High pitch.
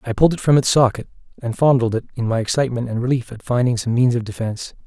No: low, 120 Hz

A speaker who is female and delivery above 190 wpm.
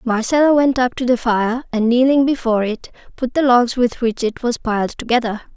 Yes: female; fast, 205 wpm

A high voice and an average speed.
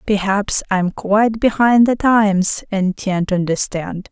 Yes: high, 200 Hz; average, 145 wpm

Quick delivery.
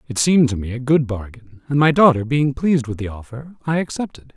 Yes: fast, 235 wpm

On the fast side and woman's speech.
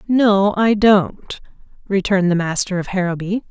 No: slow, 135 wpm; female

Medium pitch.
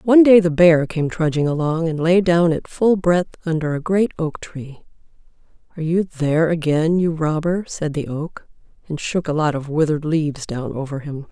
Yes: medium, 160 Hz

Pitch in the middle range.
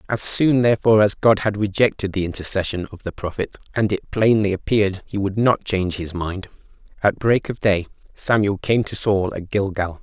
No: low, 100 Hz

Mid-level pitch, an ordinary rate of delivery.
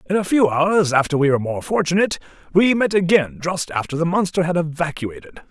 Yes: medium, 170 Hz; average, 195 wpm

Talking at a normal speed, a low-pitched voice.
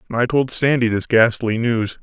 Yes: average, 180 wpm; low, 120 Hz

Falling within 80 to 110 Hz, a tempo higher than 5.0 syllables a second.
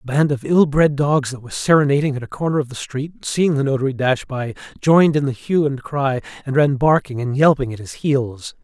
No: medium, 140 Hz; 5.6 syllables/s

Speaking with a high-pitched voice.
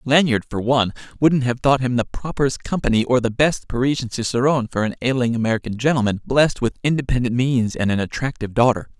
No: low, 125 Hz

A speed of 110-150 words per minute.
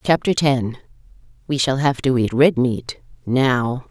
Yes: average, 140 wpm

